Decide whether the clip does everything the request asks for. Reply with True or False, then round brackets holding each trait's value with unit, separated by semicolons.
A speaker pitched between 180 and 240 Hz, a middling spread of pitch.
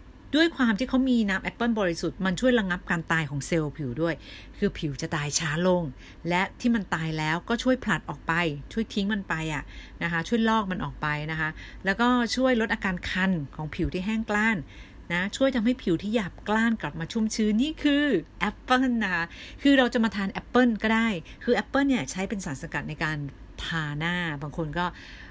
False (185 Hz; 6.1 semitones)